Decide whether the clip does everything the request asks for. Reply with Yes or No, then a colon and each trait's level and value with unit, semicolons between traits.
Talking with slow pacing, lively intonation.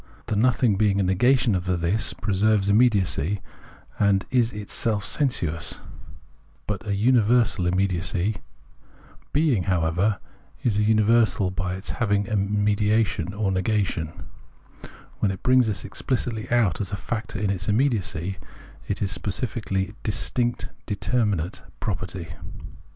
No: slow, 130 wpm; average, 3.0 semitones